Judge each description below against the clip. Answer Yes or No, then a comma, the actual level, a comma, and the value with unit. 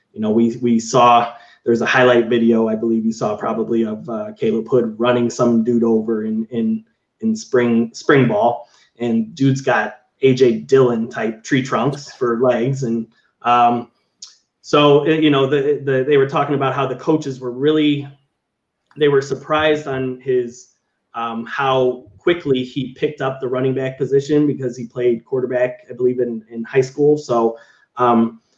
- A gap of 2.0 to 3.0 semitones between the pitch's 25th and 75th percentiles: Yes, average, 2.7 semitones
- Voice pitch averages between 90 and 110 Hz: No, low, 125 Hz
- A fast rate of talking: No, average, 170 wpm